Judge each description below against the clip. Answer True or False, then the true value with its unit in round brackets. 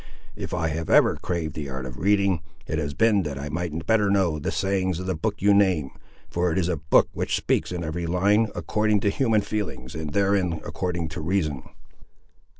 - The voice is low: True (90 Hz)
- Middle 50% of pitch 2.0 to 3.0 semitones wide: False (4.1 semitones)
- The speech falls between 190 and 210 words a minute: True (205 wpm)